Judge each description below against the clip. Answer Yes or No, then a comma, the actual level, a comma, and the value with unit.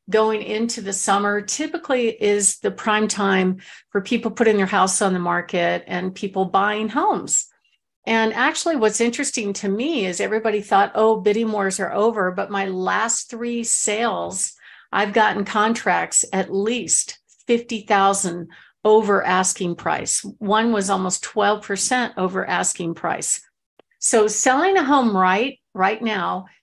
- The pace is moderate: Yes, average, 145 wpm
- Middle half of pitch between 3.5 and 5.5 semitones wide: No, average, 2.9 semitones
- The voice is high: Yes, high, 210 Hz